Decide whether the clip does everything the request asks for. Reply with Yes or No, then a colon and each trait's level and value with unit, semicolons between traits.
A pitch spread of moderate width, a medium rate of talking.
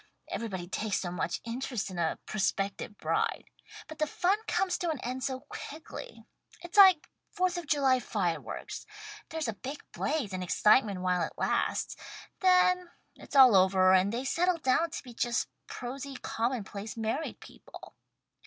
No: wide, 7.9 semitones; average, 160 wpm